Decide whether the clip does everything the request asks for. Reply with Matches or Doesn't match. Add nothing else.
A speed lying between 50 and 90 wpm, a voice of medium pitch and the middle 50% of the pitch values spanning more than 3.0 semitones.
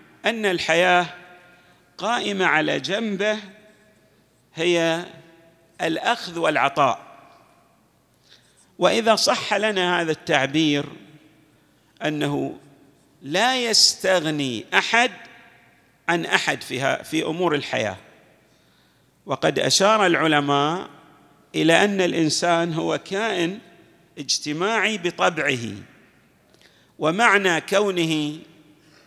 Matches